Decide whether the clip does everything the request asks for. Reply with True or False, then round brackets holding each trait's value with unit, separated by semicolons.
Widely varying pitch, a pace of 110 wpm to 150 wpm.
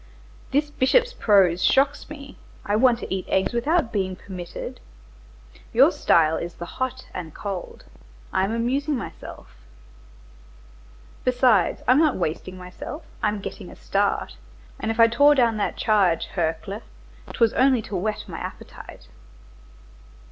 True (5.7 semitones; 140 wpm)